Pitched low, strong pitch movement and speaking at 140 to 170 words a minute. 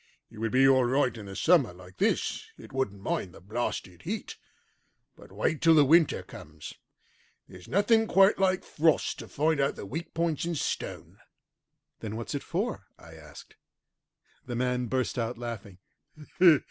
Yes: low, 125 Hz; wide, 7.6 semitones; average, 165 wpm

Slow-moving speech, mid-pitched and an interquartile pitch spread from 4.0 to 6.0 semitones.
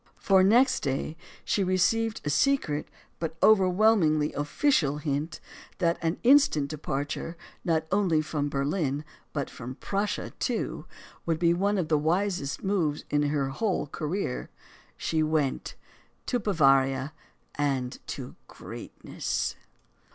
Yes: slow, 120 wpm; medium, 160 Hz; average, 5.1 semitones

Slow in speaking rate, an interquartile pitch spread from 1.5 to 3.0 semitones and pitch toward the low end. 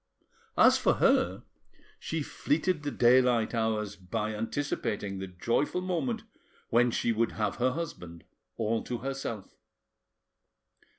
No: slow, 120 wpm; average, 4.3 semitones; low, 115 Hz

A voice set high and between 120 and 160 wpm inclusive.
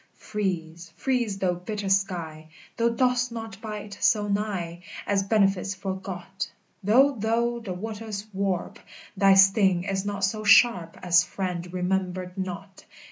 Yes: high, 195 Hz; slow, 135 wpm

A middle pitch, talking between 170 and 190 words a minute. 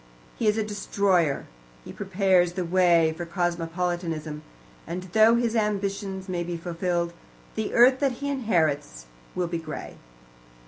No: medium, 180 Hz; average, 140 wpm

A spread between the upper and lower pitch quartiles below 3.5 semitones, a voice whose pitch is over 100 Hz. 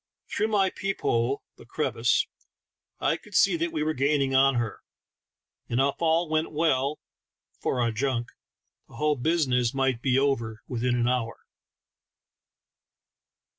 No: average, 4.2 semitones; low, 135 Hz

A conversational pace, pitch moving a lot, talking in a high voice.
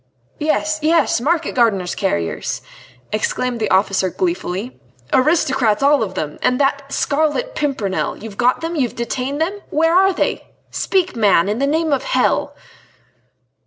Yes: average, 155 wpm; wide, 6.7 semitones; very high, 270 Hz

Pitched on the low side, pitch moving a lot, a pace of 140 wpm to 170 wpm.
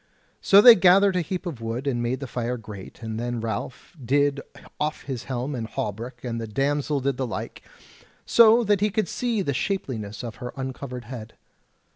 No: low, 130 Hz; wide, 6.3 semitones; average, 190 wpm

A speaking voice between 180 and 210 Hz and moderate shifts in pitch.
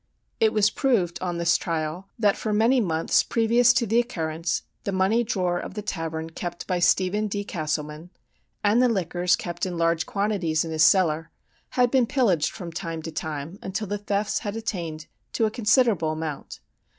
Yes: medium, 185 Hz; average, 4.7 semitones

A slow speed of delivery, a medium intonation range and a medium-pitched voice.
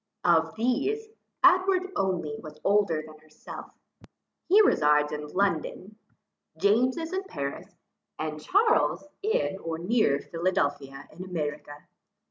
No: slow, 115 wpm; wide, 8.7 semitones; medium, 180 Hz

